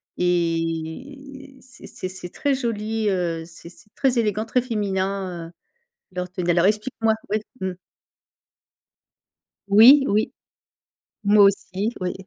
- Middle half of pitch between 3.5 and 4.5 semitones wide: Yes, average, 4.2 semitones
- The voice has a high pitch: Yes, high, 200 Hz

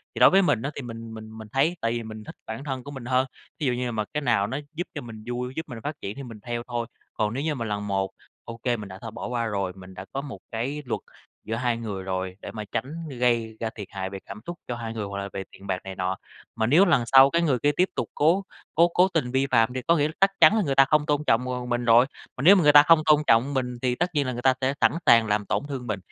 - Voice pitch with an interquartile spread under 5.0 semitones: Yes, average, 4.5 semitones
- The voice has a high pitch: No, low, 120 Hz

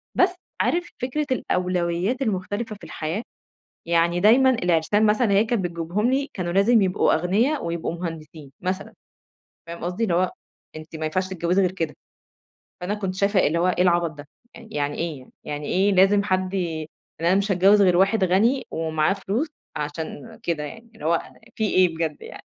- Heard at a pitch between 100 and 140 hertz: No, medium, 185 Hz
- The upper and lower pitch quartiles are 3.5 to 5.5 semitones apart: Yes, average, 3.8 semitones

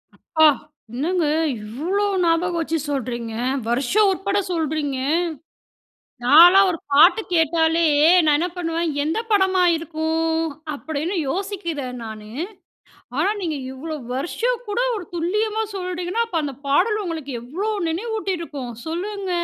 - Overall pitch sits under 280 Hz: No, very high, 330 Hz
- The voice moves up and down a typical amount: Yes, average, 4.4 semitones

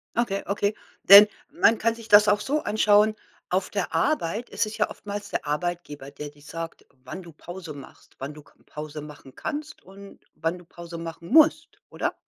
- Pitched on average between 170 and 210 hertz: Yes, high, 190 Hz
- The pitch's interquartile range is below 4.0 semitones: No, average, 4.6 semitones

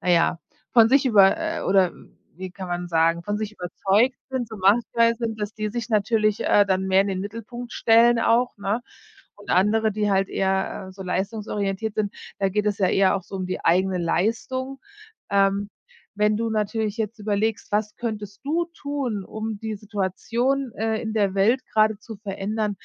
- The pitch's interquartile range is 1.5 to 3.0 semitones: Yes, narrow, 2.6 semitones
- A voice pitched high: Yes, high, 210 Hz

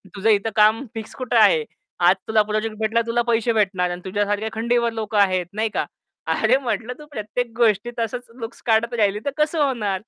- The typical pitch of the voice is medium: No, high, 220 Hz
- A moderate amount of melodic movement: No, narrow, 2.3 semitones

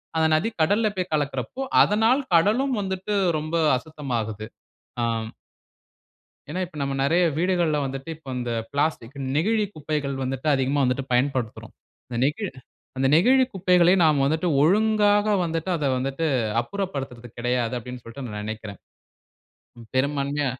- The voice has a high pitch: No, medium, 150 Hz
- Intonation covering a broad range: Yes, wide, 5.9 semitones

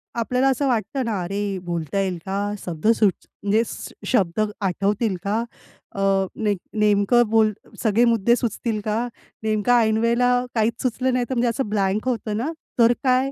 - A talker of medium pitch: No, high, 220 Hz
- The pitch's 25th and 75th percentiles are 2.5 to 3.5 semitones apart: Yes, average, 3.0 semitones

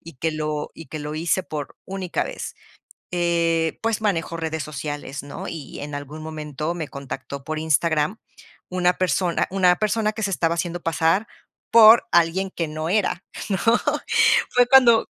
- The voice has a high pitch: No, medium, 165 Hz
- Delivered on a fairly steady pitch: No, average, 3.6 semitones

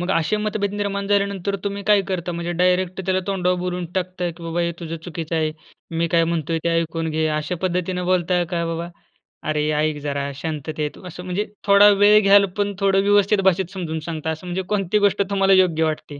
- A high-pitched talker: No, medium, 180 Hz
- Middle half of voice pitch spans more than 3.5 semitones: No, average, 3.1 semitones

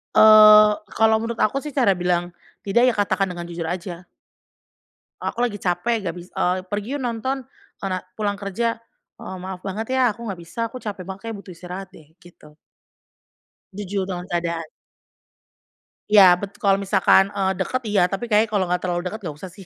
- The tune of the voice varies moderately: Yes, average, 3.3 semitones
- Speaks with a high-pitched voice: Yes, high, 195 Hz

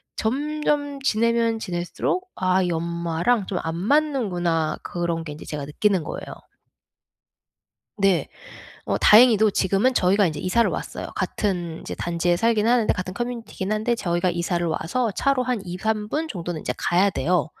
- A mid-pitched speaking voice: No, high, 195 Hz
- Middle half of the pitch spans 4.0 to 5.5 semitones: Yes, average, 5.2 semitones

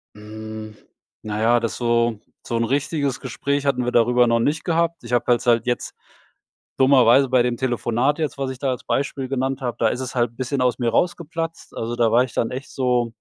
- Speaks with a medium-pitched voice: No, low, 125 Hz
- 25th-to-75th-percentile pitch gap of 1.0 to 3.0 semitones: Yes, narrow, 2.6 semitones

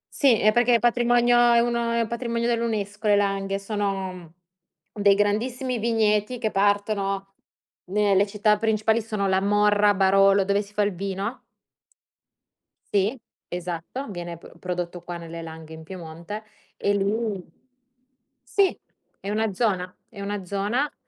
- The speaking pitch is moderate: No, high, 205 Hz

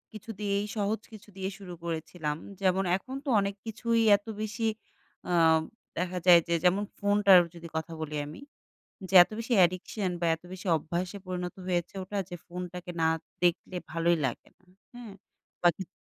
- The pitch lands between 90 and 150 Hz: No, medium, 185 Hz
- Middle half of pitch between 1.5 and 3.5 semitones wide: Yes, average, 2.8 semitones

